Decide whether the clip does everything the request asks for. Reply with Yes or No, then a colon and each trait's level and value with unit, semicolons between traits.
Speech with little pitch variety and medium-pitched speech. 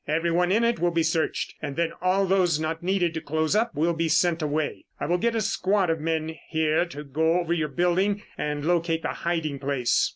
Yes: narrow, 2.3 semitones; medium, 165 Hz